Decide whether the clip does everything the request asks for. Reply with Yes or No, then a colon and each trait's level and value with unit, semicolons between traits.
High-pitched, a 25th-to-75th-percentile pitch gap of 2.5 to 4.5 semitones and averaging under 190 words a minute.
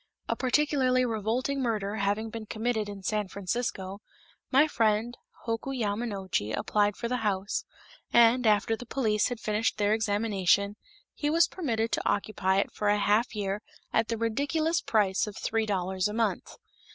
Yes: high, 220 Hz; average, 2.8 semitones; average, 160 wpm